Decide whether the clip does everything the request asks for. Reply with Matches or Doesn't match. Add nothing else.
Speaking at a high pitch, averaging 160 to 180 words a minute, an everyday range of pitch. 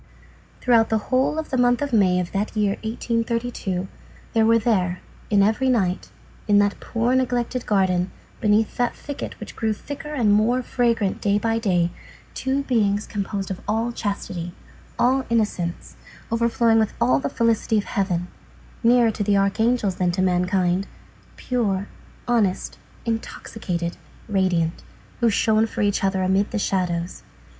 Doesn't match